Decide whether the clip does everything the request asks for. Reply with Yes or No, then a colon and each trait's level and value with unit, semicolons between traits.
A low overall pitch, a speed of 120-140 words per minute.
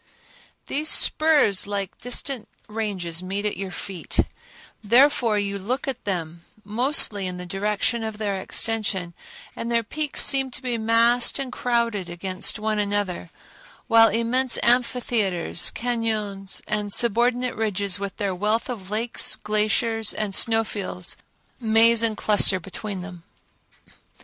No: high, 215 Hz; slow, 135 wpm